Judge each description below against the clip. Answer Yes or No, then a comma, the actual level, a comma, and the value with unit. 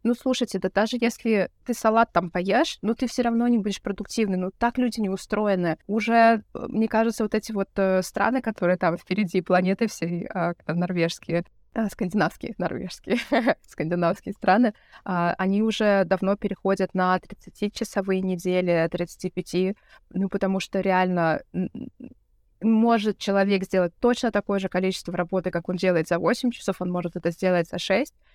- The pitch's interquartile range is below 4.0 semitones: Yes, average, 3.5 semitones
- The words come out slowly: No, fast, 160 wpm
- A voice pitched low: No, high, 195 Hz